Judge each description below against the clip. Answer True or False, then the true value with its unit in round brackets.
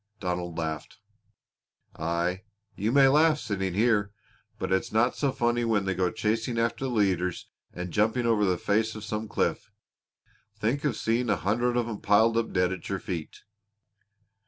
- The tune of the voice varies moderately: True (3.9 semitones)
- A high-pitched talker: False (105 Hz)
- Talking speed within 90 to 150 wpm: False (175 wpm)